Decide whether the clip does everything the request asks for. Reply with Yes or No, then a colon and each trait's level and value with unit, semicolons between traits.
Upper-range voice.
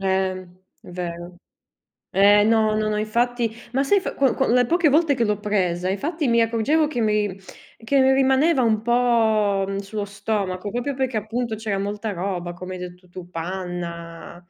Yes: high, 210 Hz